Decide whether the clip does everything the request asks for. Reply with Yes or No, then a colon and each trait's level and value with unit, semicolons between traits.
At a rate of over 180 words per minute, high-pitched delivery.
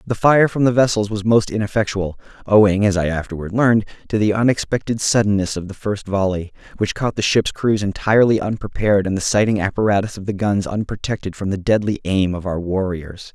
No: average, 195 wpm; low, 100 Hz